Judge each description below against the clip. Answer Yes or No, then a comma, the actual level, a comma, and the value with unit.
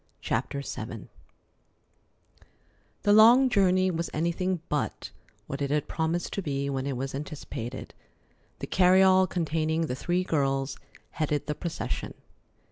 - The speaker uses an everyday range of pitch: Yes, average, 4.7 semitones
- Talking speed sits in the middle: No, slow, 125 wpm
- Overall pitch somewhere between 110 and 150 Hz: No, medium, 160 Hz